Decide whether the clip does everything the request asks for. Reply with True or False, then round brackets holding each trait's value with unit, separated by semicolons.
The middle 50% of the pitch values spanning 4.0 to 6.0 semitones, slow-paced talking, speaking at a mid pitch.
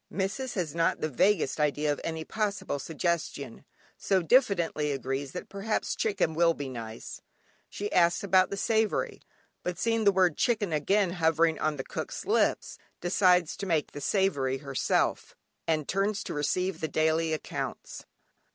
False (4.6 semitones; 150 wpm; 170 Hz)